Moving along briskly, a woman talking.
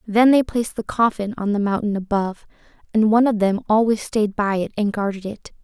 Yes: fast, 215 wpm; female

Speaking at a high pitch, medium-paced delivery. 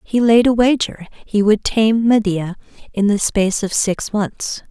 Yes: high, 210 Hz; average, 180 wpm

